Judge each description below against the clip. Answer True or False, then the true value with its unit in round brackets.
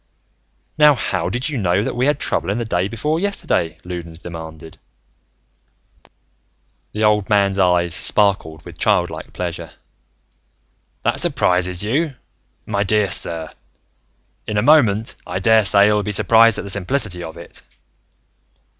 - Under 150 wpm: True (135 wpm)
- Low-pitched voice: True (100 Hz)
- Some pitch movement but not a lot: True (4.2 semitones)